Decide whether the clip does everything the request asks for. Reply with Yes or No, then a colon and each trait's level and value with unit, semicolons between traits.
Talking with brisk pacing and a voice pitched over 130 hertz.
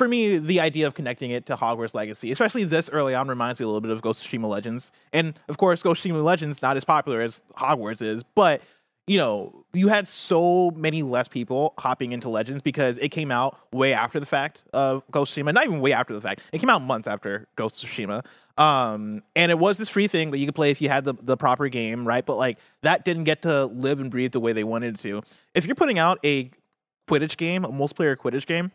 Yes: fast, 250 wpm; medium, 140 Hz